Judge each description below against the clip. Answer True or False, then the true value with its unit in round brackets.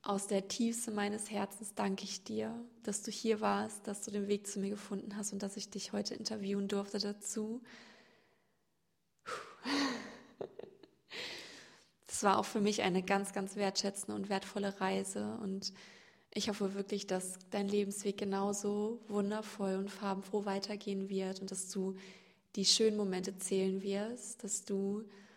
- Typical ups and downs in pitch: False (1.7 semitones)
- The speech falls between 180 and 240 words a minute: False (150 wpm)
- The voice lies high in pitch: True (205 Hz)